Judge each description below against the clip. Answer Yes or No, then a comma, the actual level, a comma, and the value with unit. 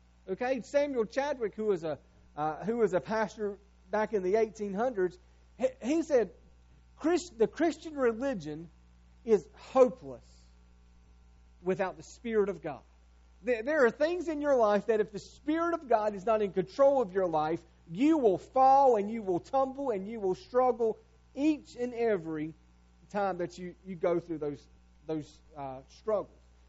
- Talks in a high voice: Yes, high, 200 Hz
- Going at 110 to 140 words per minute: No, average, 165 wpm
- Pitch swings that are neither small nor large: No, wide, 8.6 semitones